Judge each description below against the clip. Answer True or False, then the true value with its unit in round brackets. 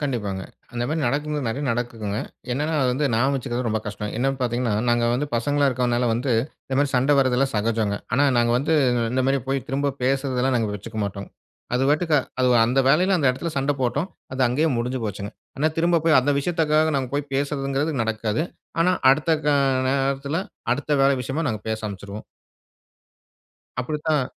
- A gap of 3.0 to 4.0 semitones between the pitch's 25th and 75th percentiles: True (3.5 semitones)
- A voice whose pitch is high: False (135 Hz)